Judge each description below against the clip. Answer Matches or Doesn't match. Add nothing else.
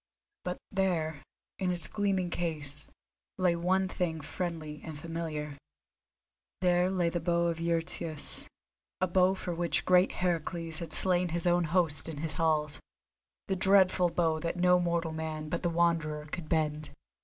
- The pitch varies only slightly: Matches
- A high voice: Doesn't match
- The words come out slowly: Doesn't match